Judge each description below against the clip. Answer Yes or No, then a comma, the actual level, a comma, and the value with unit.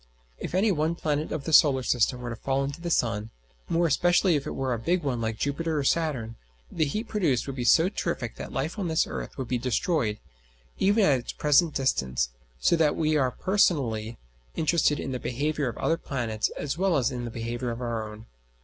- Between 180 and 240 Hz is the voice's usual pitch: No, medium, 140 Hz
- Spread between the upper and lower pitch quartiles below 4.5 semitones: No, average, 5.3 semitones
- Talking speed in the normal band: No, fast, 215 wpm